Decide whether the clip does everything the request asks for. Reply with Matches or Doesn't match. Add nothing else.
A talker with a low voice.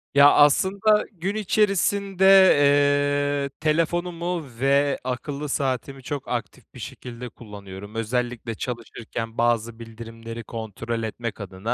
Matches